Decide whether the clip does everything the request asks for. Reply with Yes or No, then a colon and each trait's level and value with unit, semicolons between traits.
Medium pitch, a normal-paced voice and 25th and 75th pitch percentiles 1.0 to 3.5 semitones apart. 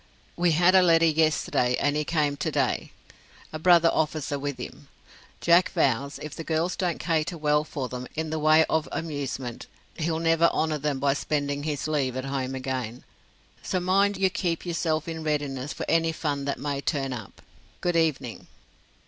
Yes: medium, 155 Hz; average, 180 wpm; average, 2.8 semitones